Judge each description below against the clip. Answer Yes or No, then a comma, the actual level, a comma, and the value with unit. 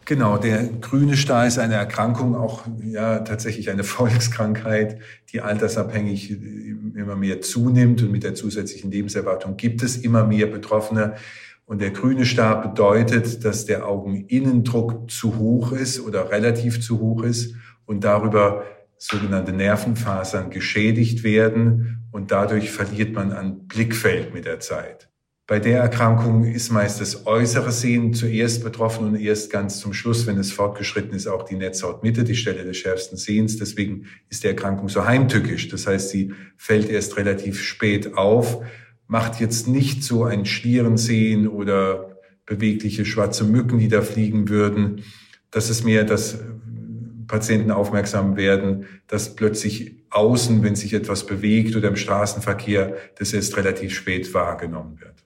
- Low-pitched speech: Yes, low, 110 Hz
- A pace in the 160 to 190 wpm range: No, average, 150 wpm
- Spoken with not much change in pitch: Yes, narrow, 2.2 semitones